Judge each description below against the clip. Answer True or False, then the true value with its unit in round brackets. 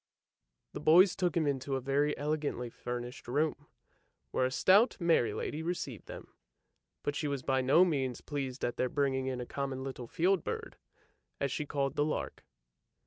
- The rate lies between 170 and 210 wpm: True (175 wpm)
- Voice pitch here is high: False (140 Hz)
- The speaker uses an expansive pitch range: False (3.0 semitones)